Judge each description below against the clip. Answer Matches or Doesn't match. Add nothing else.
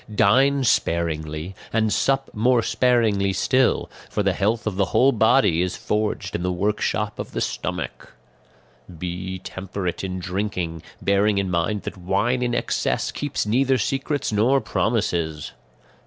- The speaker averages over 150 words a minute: Doesn't match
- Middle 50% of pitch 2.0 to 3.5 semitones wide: Doesn't match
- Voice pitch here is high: Doesn't match